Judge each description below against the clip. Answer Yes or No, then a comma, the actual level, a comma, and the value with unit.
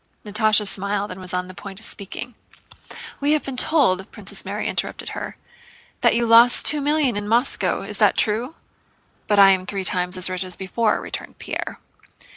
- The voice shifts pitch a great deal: No, average, 4.1 semitones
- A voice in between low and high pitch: No, high, 205 Hz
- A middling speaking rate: Yes, average, 185 wpm